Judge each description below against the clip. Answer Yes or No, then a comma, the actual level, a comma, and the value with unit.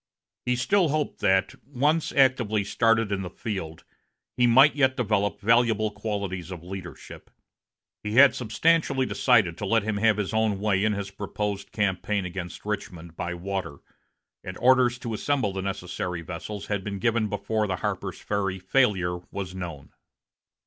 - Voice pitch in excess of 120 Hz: No, low, 105 Hz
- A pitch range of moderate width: Yes, average, 3.7 semitones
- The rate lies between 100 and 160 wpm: Yes, average, 155 wpm